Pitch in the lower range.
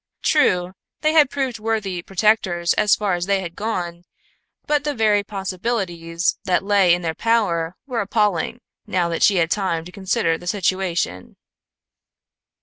No: high, 190 Hz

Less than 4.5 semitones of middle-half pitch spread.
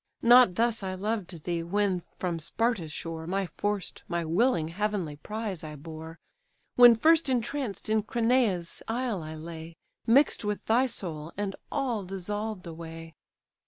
No: wide, 5.4 semitones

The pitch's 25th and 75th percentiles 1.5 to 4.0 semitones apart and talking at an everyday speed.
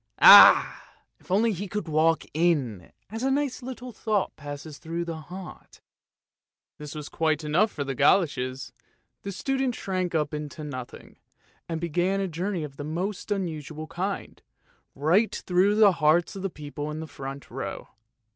No: average, 4.6 semitones; average, 165 wpm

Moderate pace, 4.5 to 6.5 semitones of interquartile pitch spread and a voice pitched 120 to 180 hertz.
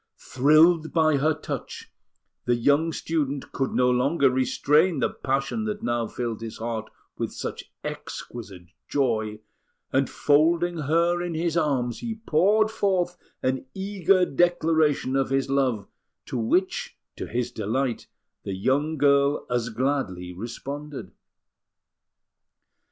No: slow, 125 wpm; average, 5.1 semitones; medium, 140 Hz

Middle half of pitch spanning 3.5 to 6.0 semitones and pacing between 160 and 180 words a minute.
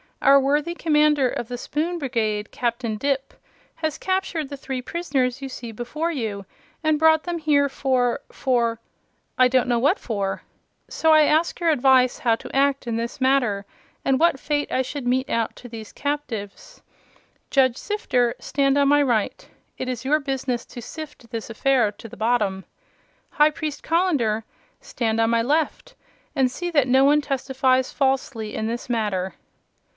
Yes: average, 3.9 semitones; average, 170 wpm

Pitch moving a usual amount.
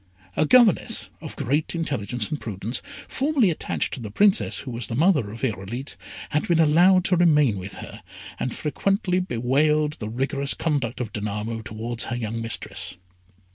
No: wide, 6.4 semitones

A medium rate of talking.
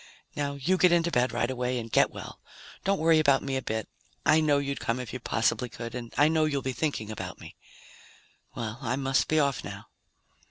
No: fast, 215 wpm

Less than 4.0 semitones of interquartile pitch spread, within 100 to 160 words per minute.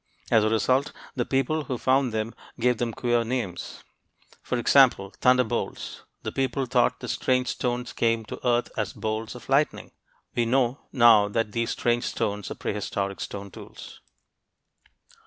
Yes: narrow, 2.6 semitones; average, 155 wpm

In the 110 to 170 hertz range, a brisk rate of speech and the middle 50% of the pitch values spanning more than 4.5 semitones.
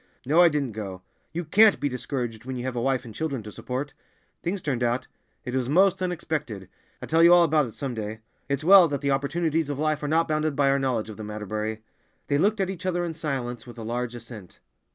Yes: medium, 140 Hz; fast, 235 wpm; average, 5.1 semitones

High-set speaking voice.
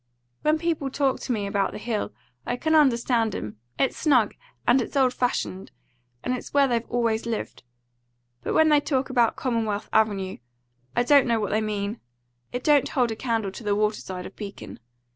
Yes: high, 235 Hz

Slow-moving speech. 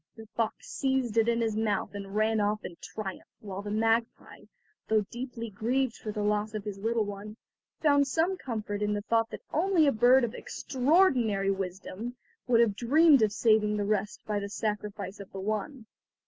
No: average, 190 wpm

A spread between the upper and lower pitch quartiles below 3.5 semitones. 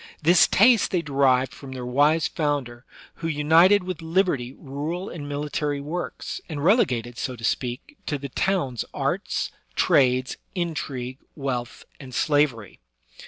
No: average, 4.3 semitones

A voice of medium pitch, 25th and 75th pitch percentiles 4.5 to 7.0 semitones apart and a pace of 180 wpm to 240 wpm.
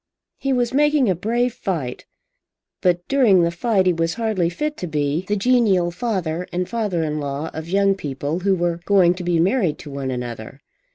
Yes: medium, 180 Hz; average, 5.2 semitones; average, 190 wpm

